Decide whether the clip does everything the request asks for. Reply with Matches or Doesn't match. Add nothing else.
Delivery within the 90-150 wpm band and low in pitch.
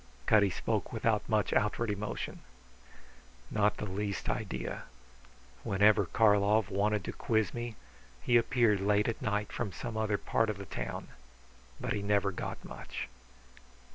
Matches